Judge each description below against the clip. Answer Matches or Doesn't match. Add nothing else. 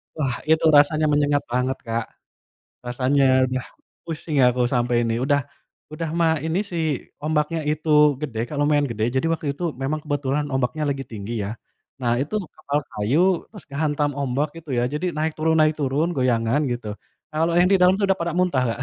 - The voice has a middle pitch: Matches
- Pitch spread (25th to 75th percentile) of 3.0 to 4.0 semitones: Matches